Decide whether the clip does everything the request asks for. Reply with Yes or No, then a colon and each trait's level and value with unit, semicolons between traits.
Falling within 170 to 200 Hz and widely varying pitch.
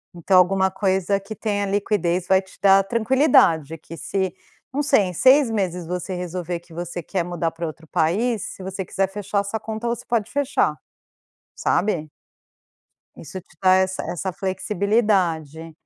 No: high, 190 Hz; average, 3.1 semitones